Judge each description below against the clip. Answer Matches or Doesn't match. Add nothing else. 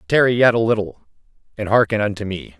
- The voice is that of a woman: Doesn't match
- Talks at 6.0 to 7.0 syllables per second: Matches